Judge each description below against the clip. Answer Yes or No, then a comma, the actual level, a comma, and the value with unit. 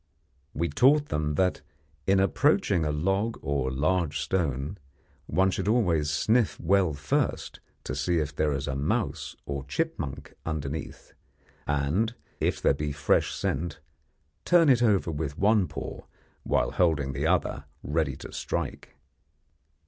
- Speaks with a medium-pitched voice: No, very low, 80 Hz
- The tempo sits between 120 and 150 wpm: Yes, average, 140 wpm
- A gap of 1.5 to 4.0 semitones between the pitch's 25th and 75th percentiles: No, average, 5.1 semitones